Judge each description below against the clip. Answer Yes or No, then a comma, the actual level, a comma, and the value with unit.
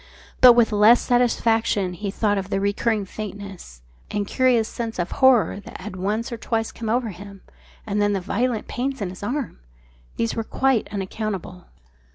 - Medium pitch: No, high, 215 Hz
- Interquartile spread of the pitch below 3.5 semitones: Yes, average, 2.9 semitones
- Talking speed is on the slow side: No, average, 180 wpm